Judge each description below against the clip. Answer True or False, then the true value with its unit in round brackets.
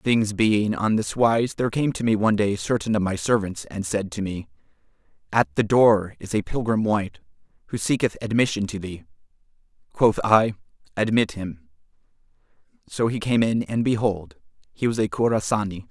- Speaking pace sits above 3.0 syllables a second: True (5.0 syllables/s)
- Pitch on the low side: True (105 Hz)